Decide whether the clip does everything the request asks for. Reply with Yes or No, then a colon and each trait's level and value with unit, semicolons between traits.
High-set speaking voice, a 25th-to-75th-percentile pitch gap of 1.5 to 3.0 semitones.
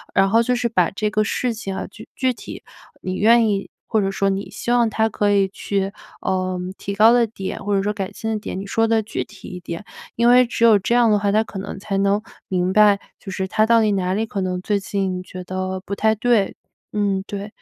Yes: high, 205 Hz; narrow, 2.4 semitones